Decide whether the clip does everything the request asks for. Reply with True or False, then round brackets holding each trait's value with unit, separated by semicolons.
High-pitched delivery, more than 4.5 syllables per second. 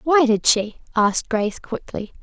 True (235 Hz; 4.8 syllables/s)